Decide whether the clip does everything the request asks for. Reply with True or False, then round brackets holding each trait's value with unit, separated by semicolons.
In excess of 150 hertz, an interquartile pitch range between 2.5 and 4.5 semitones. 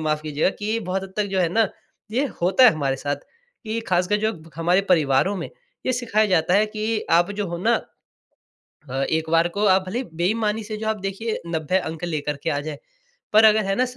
False (190 Hz; 5.1 semitones)